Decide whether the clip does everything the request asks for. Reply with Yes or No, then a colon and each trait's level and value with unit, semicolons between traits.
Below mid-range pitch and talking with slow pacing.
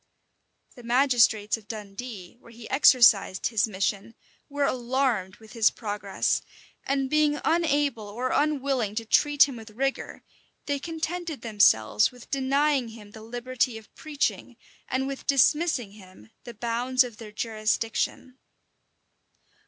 No: high, 240 Hz; slow, 130 wpm